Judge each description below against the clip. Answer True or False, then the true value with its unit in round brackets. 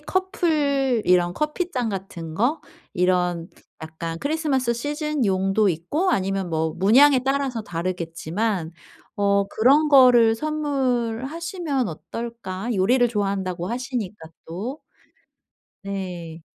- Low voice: False (225 Hz)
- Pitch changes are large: True (7.1 semitones)